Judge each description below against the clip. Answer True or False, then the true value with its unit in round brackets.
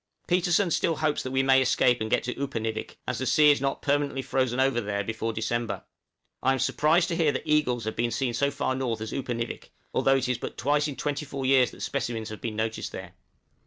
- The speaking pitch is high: False (130 Hz)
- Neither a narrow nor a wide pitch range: True (3.6 semitones)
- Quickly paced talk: True (225 wpm)